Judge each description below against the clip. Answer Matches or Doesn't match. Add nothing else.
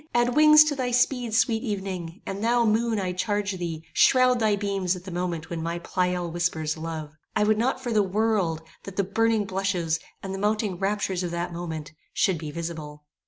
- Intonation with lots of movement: Doesn't match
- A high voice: Matches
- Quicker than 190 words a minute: Matches